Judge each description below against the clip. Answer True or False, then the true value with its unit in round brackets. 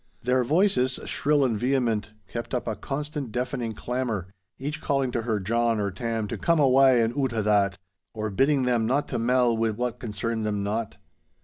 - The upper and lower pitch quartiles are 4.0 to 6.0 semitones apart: False (3.2 semitones)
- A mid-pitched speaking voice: False (120 Hz)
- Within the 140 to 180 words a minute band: False (190 wpm)